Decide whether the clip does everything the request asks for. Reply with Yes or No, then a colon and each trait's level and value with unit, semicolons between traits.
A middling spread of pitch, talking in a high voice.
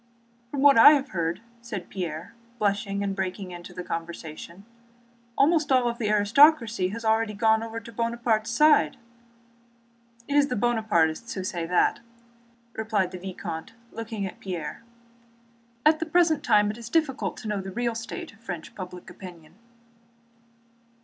Yes: average, 4.4 semitones; high, 215 Hz